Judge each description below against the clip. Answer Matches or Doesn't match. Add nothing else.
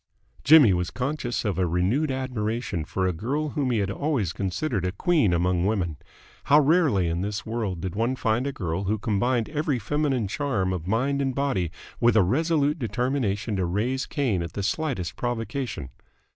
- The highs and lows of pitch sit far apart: Matches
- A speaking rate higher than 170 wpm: Matches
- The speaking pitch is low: Matches